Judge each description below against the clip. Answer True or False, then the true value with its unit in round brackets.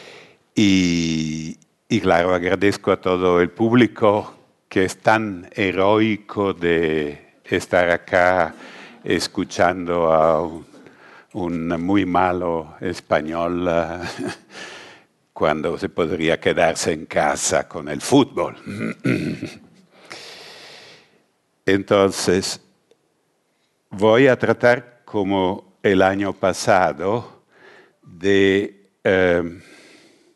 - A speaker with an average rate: False (80 wpm)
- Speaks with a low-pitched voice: True (95 Hz)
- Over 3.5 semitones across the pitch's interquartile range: False (3.2 semitones)